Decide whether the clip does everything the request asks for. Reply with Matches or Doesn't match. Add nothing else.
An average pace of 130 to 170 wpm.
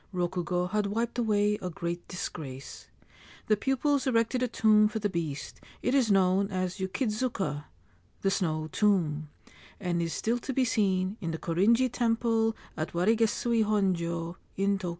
Matches